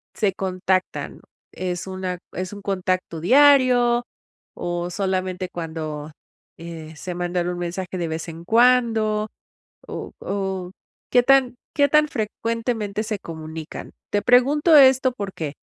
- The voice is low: No, high, 190 Hz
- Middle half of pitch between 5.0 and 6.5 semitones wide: Yes, average, 5.3 semitones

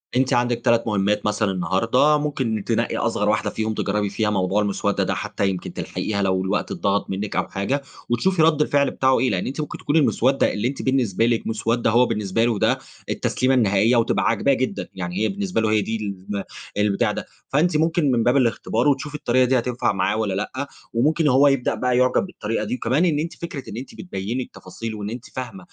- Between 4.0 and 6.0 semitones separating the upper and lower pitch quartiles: Yes, average, 4.6 semitones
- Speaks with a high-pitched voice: No, low, 120 Hz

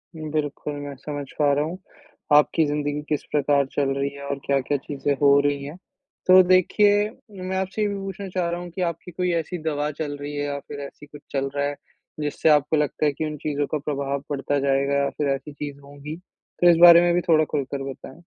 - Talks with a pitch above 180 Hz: No, medium, 145 Hz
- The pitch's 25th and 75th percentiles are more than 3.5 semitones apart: No, average, 3.0 semitones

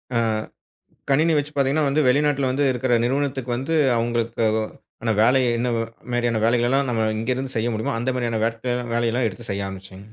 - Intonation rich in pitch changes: No, average, 2.9 semitones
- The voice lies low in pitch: Yes, low, 120 Hz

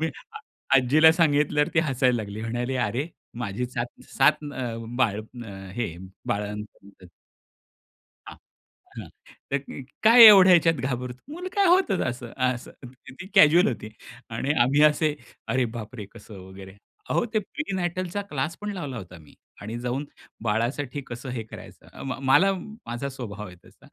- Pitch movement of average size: No, wide, 6.0 semitones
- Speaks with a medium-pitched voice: No, low, 130 Hz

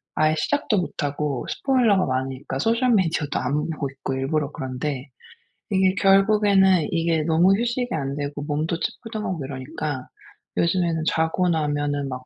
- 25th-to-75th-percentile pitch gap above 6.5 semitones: No, average, 5.1 semitones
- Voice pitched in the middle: Yes, medium, 160 Hz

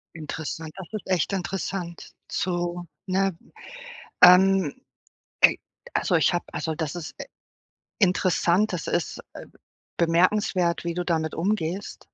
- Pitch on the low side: No, medium, 175 Hz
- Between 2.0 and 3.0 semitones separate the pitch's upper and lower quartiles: Yes, narrow, 2.4 semitones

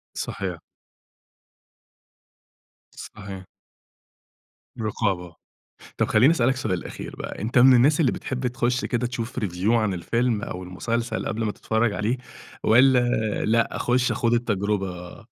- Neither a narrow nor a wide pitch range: Yes, average, 3.3 semitones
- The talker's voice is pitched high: No, low, 115 Hz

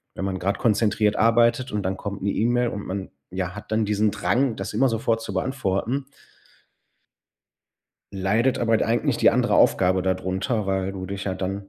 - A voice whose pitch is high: No, low, 100 Hz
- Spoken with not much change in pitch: No, average, 3.1 semitones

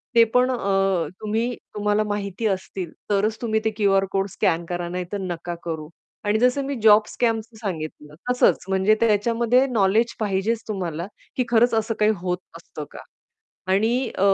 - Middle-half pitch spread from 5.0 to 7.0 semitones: No, average, 3.3 semitones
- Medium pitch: No, high, 210 Hz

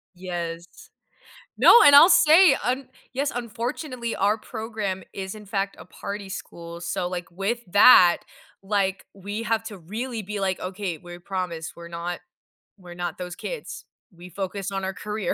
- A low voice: No, high, 195 Hz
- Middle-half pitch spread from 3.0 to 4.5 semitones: Yes, average, 4.0 semitones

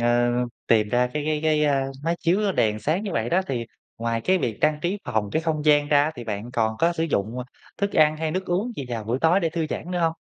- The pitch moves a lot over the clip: Yes, wide, 5.9 semitones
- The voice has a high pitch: No, medium, 150 Hz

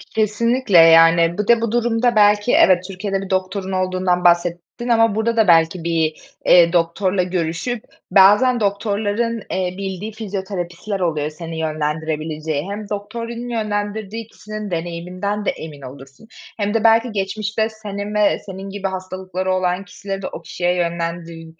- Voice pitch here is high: Yes, high, 195 Hz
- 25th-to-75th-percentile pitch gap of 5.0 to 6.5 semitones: No, average, 3.7 semitones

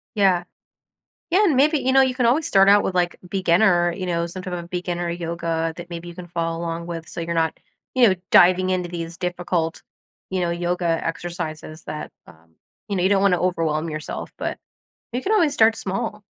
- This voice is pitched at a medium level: Yes, medium, 175 Hz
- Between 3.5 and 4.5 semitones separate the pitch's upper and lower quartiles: No, narrow, 2.5 semitones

